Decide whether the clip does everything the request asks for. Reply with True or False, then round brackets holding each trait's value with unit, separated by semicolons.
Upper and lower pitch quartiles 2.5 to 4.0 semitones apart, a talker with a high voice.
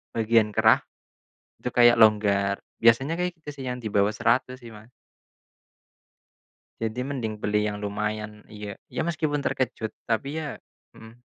False (3.0 semitones; 115 Hz)